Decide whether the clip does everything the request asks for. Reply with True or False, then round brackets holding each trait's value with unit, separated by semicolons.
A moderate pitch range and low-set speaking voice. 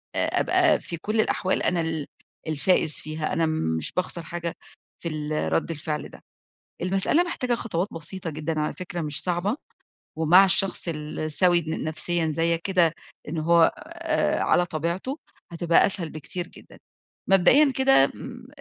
False (3.5 semitones; 170 Hz)